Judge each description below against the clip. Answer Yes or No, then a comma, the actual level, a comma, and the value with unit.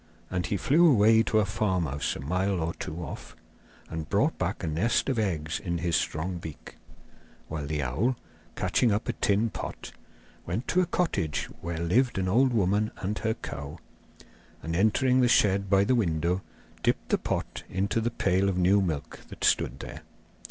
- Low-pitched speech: Yes, very low, 95 Hz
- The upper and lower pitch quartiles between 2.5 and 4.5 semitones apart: No, average, 5.1 semitones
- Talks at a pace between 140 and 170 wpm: No, average, 180 wpm